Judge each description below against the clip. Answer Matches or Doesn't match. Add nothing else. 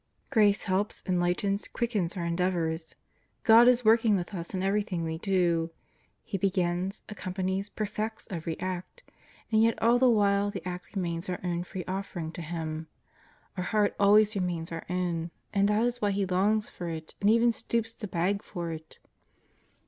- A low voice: Doesn't match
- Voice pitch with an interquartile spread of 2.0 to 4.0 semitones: Matches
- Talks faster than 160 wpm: Matches